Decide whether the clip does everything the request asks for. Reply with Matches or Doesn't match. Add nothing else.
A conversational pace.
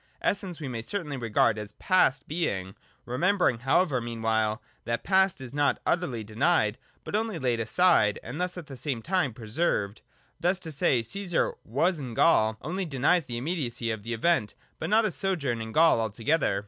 Matches